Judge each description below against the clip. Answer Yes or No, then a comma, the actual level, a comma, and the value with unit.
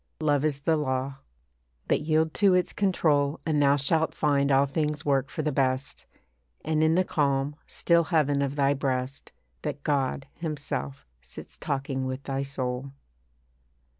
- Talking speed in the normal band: Yes, average, 155 wpm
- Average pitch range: No, narrow, 2.3 semitones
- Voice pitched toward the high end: No, medium, 145 Hz